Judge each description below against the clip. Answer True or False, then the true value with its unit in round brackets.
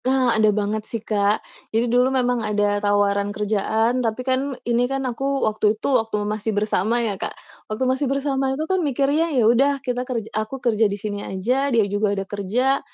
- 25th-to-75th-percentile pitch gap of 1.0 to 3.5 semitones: False (4.0 semitones)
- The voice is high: True (230 Hz)